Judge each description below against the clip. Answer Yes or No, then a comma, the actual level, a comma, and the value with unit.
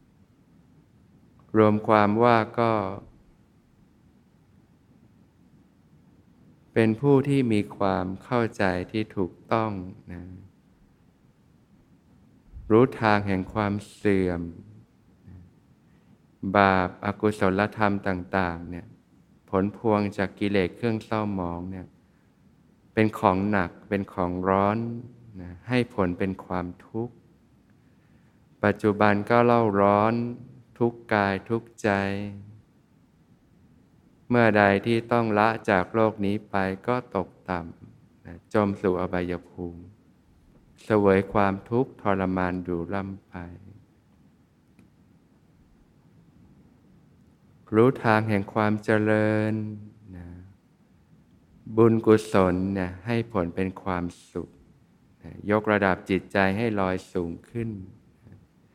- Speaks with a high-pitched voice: No, low, 100 Hz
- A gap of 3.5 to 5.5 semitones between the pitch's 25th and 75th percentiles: No, average, 3.1 semitones